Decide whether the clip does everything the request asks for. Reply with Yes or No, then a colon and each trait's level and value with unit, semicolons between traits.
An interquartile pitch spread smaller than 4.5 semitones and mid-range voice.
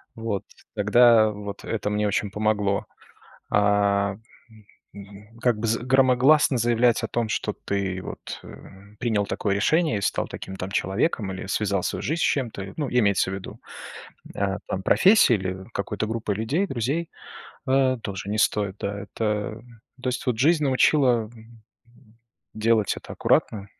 No: average, 3.7 semitones; low, 110 Hz